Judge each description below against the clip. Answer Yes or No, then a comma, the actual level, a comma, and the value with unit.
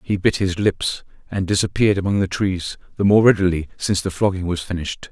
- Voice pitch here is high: No, very low, 95 Hz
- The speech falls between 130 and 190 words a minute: No, average, 200 wpm